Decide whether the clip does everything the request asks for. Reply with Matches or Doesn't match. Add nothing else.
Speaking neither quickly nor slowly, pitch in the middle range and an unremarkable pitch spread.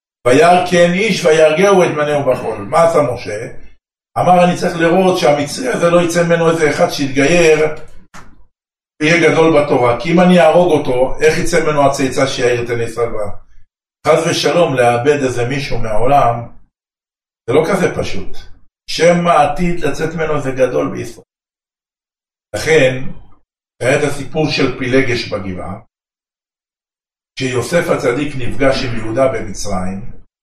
Doesn't match